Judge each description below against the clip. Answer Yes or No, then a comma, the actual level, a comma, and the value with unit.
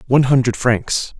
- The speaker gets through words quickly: No, average, 150 wpm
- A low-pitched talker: Yes, low, 125 Hz